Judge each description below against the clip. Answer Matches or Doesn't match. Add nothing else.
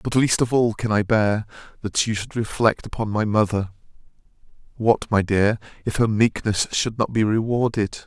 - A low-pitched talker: Matches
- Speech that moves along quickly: Doesn't match